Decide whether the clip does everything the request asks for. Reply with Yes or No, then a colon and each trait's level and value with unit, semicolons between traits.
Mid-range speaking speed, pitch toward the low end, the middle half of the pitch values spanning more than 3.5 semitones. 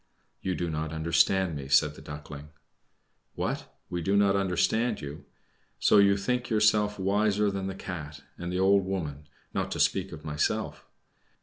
Yes: average, 165 wpm; very low, 95 Hz; average, 4.5 semitones